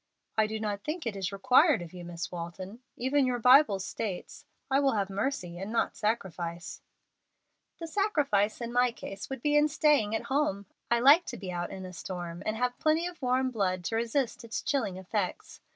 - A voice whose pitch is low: No, high, 225 Hz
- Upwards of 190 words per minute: Yes, average, 200 wpm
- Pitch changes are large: Yes, wide, 6.0 semitones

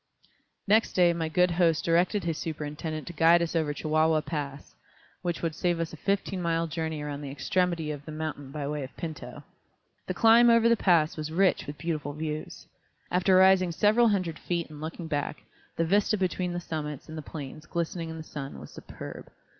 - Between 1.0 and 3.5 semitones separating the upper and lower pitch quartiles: Yes, average, 2.7 semitones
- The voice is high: No, medium, 165 Hz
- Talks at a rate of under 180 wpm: No, average, 195 wpm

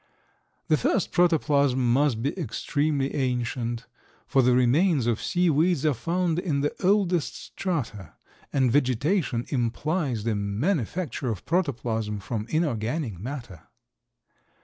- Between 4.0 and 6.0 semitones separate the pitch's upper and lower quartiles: Yes, wide, 5.5 semitones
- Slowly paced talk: Yes, slow, 120 wpm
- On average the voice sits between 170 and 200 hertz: No, low, 135 Hz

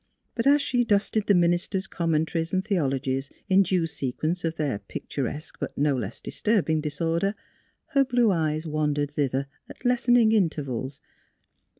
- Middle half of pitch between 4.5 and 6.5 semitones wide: Yes, wide, 5.5 semitones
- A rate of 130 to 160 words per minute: Yes, average, 150 wpm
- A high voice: No, medium, 165 Hz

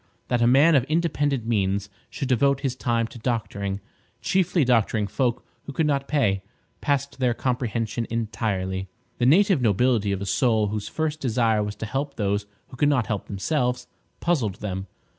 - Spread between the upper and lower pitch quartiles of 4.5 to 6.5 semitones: Yes, average, 4.9 semitones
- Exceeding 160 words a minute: Yes, average, 170 wpm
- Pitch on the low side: Yes, low, 120 Hz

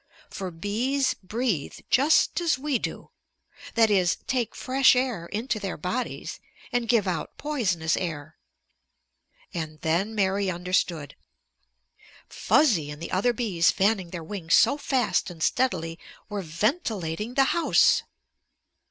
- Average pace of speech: No, slow, 125 wpm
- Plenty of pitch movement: Yes, wide, 6.5 semitones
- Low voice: No, high, 200 Hz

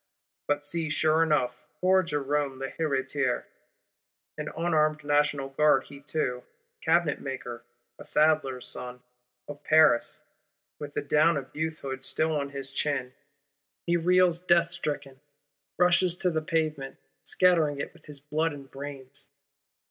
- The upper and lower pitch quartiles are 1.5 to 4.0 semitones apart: Yes, average, 2.7 semitones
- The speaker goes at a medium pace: No, slow, 130 wpm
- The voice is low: No, medium, 150 Hz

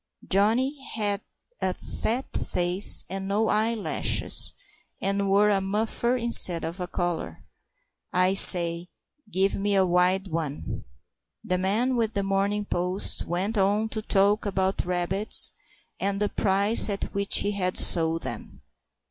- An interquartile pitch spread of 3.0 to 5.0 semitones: No, narrow, 2.4 semitones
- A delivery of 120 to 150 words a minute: Yes, average, 140 wpm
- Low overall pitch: No, high, 195 Hz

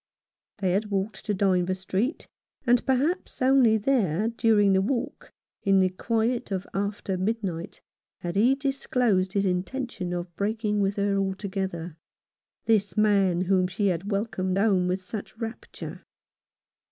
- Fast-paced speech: No, average, 140 wpm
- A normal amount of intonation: Yes, average, 3.1 semitones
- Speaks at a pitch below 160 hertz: No, high, 200 Hz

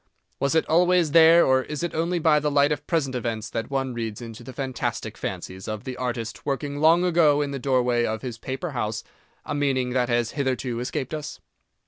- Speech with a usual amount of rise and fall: Yes, average, 3.8 semitones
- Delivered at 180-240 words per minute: Yes, fast, 205 wpm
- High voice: No, low, 135 Hz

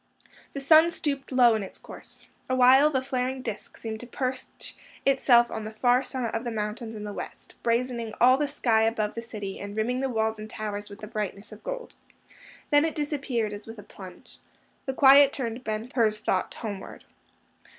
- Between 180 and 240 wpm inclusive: Yes, average, 190 wpm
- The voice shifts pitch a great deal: No, average, 3.5 semitones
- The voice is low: No, high, 235 Hz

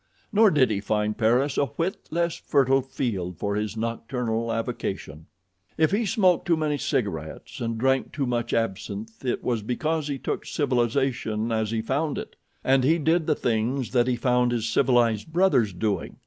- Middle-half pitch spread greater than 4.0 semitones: Yes, average, 4.4 semitones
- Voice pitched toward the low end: Yes, low, 120 Hz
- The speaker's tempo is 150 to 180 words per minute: Yes, average, 170 wpm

